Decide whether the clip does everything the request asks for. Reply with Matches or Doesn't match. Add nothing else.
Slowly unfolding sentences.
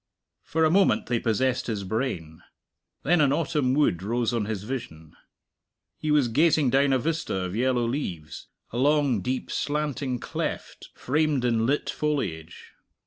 Doesn't match